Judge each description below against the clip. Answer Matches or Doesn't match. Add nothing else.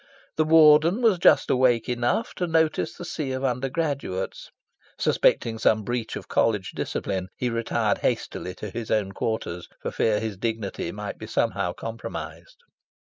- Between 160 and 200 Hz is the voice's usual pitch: Doesn't match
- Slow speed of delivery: Doesn't match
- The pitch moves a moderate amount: Doesn't match